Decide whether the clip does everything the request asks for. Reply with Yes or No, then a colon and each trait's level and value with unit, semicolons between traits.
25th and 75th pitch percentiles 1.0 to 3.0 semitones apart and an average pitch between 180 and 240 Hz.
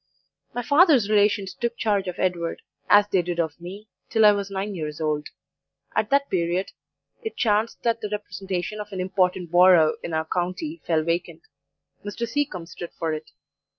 No: average, 3.7 semitones; high, 190 Hz